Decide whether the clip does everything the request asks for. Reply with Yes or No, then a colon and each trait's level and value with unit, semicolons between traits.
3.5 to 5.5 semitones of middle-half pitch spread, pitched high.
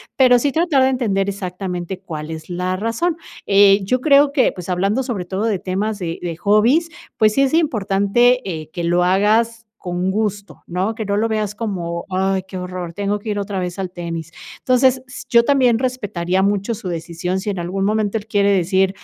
Yes: average, 3.9 semitones; high, 200 Hz